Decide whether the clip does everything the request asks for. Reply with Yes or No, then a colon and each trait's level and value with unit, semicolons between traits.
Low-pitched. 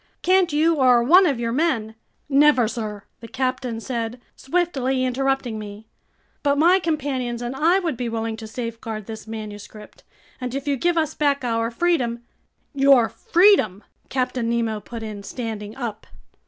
No: very high, 250 Hz